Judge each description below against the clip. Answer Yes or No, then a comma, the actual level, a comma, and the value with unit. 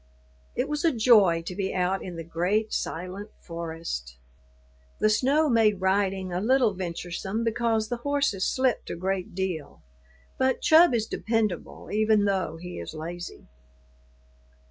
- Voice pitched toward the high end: Yes, high, 195 Hz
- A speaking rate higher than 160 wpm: No, average, 145 wpm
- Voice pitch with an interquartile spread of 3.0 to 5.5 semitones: Yes, average, 4.5 semitones